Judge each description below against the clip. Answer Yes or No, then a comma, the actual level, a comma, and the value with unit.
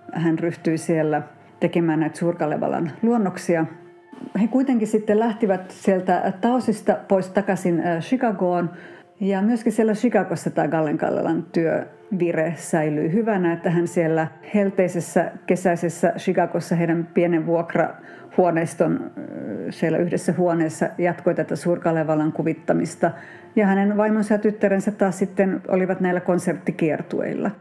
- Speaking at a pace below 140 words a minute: Yes, average, 115 wpm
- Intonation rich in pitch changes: No, average, 3.6 semitones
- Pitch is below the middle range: No, medium, 180 Hz